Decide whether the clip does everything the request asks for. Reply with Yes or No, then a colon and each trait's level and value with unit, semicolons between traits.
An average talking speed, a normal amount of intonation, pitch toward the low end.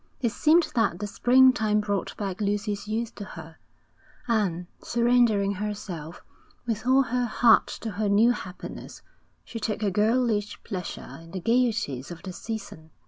No: average, 150 wpm; average, 3.2 semitones; high, 210 Hz